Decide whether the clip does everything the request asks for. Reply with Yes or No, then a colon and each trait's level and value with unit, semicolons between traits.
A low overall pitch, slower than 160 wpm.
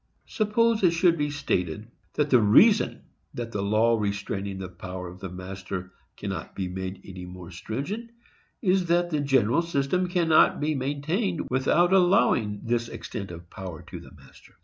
No: low, 120 Hz; average, 165 wpm